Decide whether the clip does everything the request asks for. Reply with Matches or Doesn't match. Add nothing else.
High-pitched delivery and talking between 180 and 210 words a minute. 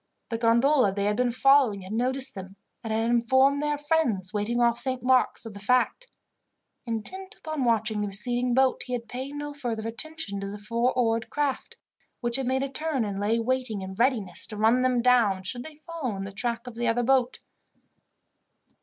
Matches